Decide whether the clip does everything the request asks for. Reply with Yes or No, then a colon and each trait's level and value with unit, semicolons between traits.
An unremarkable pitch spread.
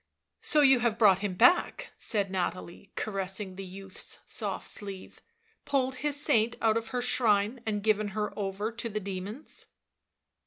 Yes: average, 3.4 semitones